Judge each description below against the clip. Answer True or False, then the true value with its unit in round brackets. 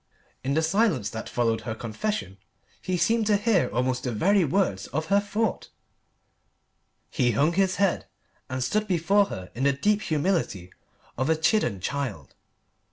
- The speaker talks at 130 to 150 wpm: False (160 wpm)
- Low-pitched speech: False (155 Hz)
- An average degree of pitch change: False (8.6 semitones)